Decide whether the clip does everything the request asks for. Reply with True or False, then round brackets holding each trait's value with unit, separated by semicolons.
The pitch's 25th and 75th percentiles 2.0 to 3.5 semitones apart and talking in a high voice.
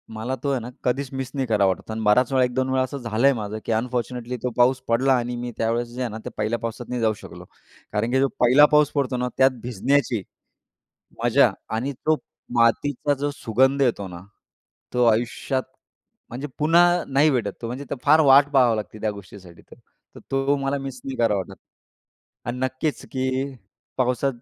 False (2.8 semitones; 125 Hz)